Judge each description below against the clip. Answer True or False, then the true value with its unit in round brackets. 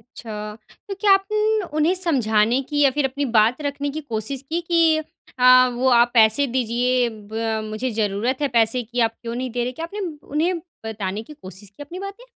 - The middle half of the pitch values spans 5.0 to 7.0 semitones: True (5.6 semitones)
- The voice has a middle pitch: False (255 Hz)